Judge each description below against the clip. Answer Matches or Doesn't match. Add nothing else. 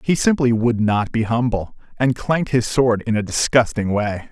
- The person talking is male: Matches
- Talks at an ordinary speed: Matches